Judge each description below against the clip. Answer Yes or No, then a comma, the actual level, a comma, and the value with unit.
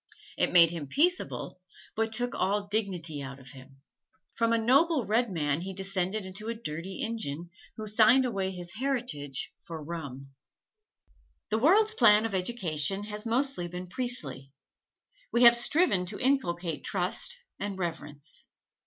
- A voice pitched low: No, high, 195 Hz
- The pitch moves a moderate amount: No, wide, 5.8 semitones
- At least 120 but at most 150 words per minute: Yes, average, 145 wpm